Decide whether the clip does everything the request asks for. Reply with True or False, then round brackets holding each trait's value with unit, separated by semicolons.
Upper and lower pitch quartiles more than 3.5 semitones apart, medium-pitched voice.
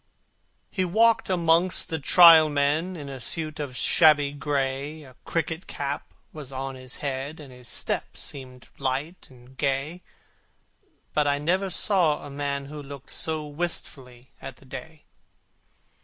False (3.1 semitones; 145 Hz)